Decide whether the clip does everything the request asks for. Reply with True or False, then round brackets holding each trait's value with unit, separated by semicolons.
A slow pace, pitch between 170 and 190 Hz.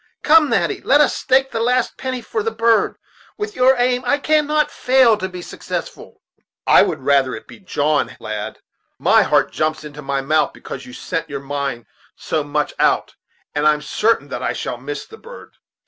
False (195 wpm; 185 Hz)